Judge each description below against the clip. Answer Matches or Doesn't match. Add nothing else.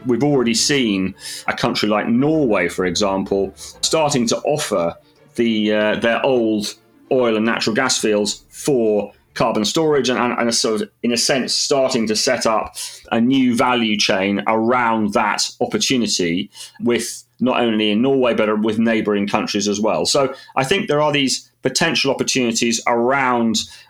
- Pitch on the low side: Matches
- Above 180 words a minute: Doesn't match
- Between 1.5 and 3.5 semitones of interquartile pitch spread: Matches